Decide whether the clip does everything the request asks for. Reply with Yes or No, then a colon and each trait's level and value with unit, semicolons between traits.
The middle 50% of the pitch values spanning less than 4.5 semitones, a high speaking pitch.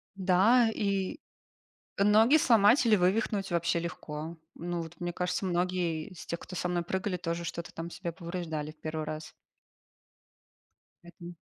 No: average, 2.7 semitones; medium, 175 Hz